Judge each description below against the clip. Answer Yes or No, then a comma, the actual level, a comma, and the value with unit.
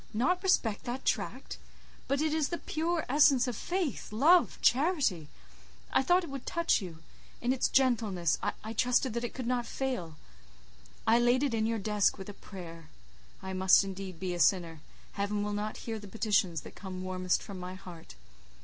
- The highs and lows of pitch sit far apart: Yes, wide, 6.0 semitones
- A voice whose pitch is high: Yes, high, 220 Hz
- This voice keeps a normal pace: Yes, average, 185 wpm